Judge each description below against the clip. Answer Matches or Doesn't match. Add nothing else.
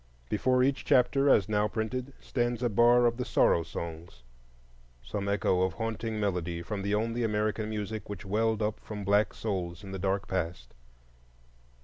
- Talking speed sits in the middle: Matches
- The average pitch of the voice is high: Doesn't match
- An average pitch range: Matches